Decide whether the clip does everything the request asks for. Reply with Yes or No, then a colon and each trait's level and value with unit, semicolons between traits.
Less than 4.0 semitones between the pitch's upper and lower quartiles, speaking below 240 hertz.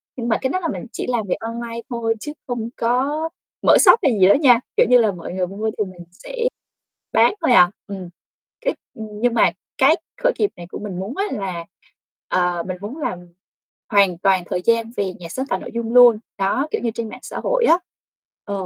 No: average, 4.6 semitones; high, 225 Hz